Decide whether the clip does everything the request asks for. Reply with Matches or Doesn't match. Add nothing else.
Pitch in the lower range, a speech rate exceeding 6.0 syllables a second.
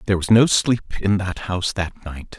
Doesn't match